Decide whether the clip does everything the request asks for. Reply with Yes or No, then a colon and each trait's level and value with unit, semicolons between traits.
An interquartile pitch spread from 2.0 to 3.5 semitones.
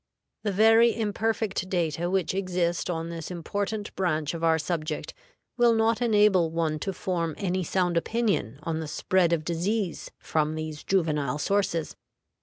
No: average, 3.9 semitones